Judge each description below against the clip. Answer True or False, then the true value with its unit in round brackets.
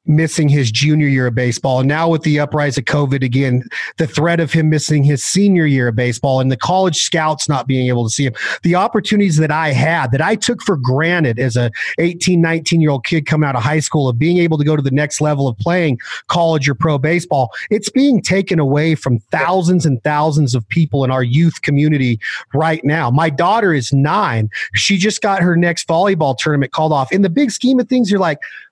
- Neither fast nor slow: False (225 wpm)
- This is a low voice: False (155 Hz)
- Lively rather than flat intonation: False (3.9 semitones)